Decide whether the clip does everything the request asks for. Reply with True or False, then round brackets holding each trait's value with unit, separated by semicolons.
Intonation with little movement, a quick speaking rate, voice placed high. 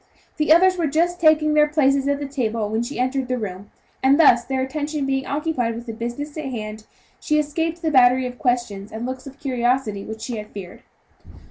False (4.3 semitones; 210 wpm; 265 Hz)